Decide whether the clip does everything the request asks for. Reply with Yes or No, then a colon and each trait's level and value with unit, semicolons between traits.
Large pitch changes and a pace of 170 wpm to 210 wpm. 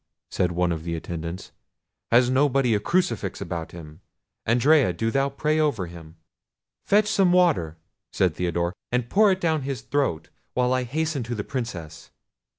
No: wide, 9.0 semitones; average, 160 wpm